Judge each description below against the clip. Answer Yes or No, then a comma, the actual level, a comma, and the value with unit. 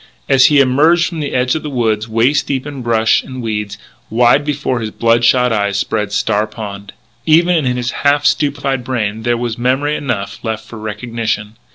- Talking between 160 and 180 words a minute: No, average, 190 wpm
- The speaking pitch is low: Yes, low, 120 Hz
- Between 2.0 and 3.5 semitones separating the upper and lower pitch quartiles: No, average, 4.0 semitones